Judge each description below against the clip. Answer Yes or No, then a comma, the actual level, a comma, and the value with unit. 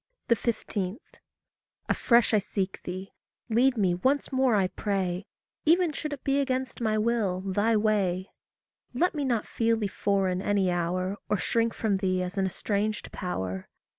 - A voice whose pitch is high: Yes, high, 205 Hz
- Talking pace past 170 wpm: No, average, 155 wpm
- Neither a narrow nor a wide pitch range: Yes, average, 3.9 semitones